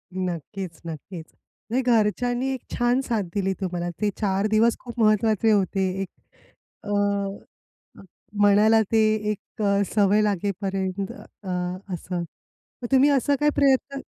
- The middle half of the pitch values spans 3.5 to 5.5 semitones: Yes, average, 3.8 semitones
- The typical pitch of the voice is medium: No, high, 205 Hz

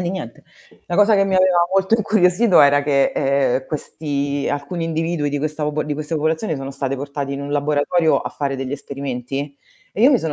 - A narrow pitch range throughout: No, average, 3.7 semitones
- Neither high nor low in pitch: Yes, medium, 150 Hz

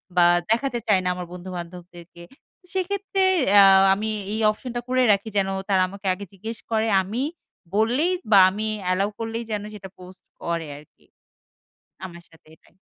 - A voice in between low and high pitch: No, high, 200 Hz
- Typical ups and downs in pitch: Yes, average, 3.9 semitones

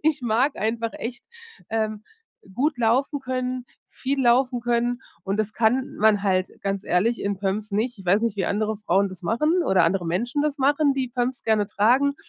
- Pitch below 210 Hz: No, high, 230 Hz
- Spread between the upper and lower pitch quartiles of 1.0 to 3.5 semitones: No, average, 4.0 semitones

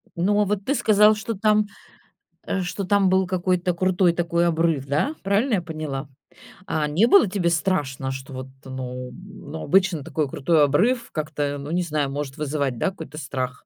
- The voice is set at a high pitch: No, medium, 170 Hz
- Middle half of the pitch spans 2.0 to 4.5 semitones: No, average, 5.2 semitones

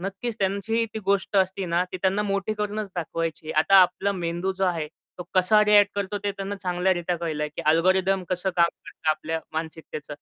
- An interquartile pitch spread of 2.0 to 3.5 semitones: Yes, average, 2.9 semitones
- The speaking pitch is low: No, medium, 185 Hz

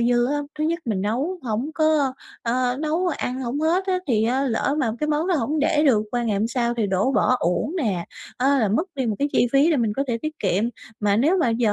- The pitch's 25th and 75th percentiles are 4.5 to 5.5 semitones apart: Yes, average, 5.0 semitones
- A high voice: Yes, very high, 255 Hz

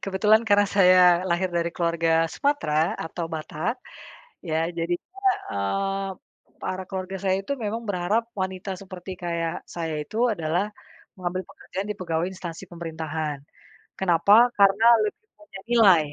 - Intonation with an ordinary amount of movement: Yes, average, 3.2 semitones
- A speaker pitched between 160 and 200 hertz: Yes, medium, 185 Hz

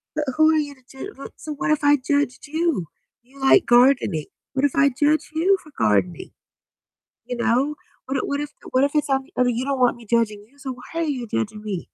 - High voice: Yes, very high, 270 Hz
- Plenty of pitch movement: No, average, 3.4 semitones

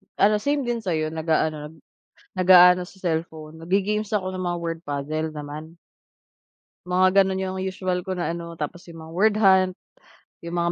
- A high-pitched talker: No, medium, 175 Hz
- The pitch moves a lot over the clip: No, average, 2.8 semitones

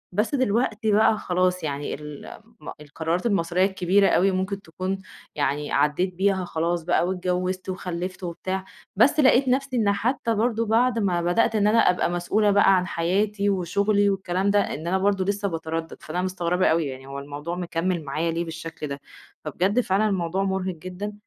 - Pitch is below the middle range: No, medium, 185 Hz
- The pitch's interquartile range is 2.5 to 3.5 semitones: Yes, average, 3.2 semitones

